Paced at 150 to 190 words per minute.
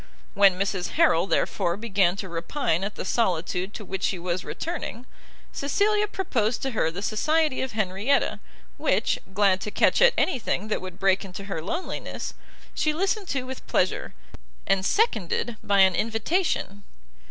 Yes: average, 160 wpm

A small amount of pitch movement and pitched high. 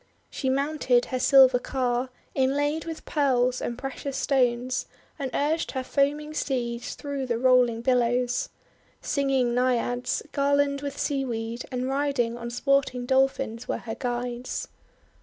Yes: narrow, 2.3 semitones; very high, 255 Hz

